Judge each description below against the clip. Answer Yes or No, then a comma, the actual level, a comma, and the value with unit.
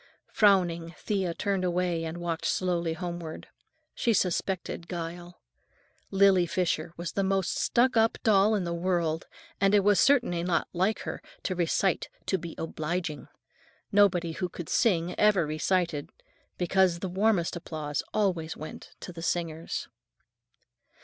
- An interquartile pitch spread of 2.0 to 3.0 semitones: Yes, narrow, 2.5 semitones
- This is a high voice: No, medium, 175 Hz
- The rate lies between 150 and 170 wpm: No, average, 140 wpm